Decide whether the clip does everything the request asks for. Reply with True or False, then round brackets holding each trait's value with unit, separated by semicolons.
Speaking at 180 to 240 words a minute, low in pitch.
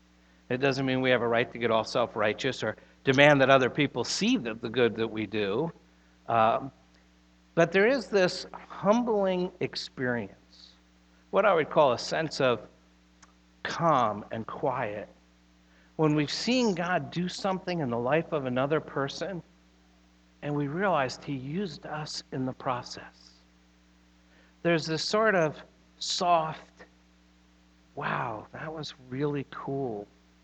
False (140 wpm; 125 Hz)